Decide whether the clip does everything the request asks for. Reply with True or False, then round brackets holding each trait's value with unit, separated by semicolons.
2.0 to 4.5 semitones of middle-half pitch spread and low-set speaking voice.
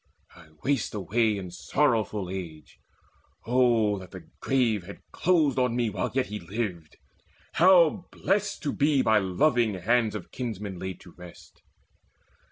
False (5.5 semitones; 110 Hz)